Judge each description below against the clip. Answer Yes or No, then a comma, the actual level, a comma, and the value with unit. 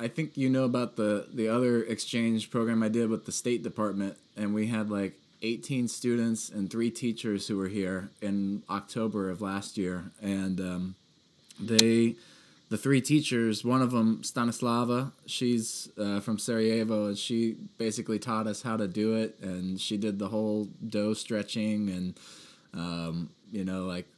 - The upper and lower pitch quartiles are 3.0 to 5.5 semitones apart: No, narrow, 2.6 semitones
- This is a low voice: Yes, low, 110 Hz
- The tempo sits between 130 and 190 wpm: Yes, average, 170 wpm